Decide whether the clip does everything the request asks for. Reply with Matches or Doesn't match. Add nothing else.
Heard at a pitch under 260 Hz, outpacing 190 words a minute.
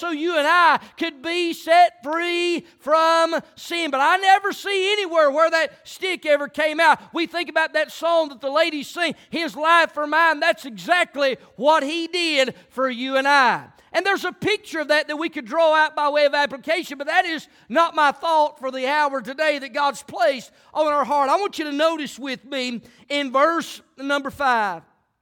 Doesn't match